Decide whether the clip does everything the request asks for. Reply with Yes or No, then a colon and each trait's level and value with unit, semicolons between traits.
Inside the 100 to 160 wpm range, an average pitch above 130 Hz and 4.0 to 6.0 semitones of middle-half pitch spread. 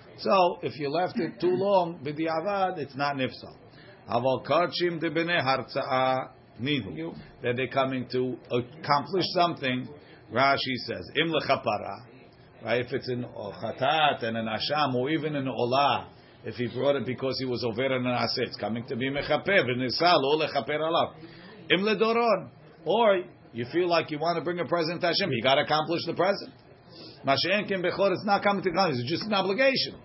No: average, 170 wpm; medium, 140 Hz; average, 5.2 semitones